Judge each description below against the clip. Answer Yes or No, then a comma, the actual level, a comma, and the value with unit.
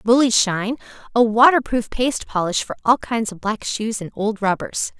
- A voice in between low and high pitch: No, high, 225 Hz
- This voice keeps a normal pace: Yes, average, 180 wpm